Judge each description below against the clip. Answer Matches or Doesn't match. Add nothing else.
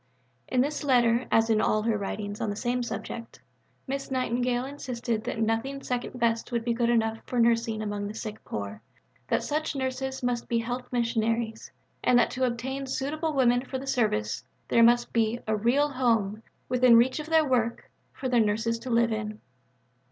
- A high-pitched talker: Matches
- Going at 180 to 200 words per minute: Matches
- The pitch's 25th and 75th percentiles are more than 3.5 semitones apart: Doesn't match